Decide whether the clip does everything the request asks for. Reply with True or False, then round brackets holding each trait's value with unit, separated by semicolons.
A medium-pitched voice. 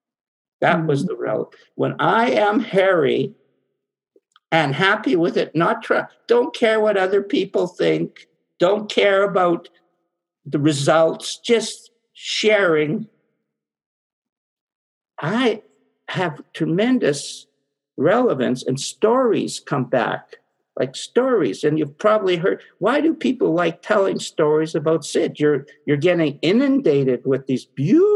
True (180 Hz)